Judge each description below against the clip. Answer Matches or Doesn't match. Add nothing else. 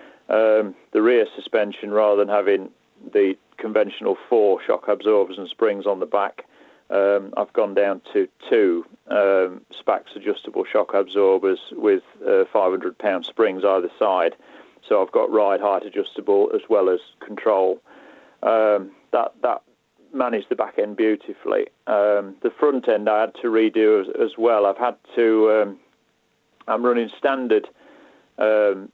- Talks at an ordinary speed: Matches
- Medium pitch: Matches